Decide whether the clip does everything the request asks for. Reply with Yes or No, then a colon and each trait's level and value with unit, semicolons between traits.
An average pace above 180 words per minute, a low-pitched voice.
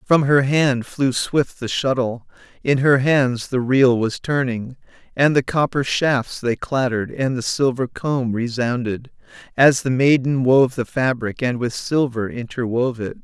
No: average, 165 wpm; low, 130 Hz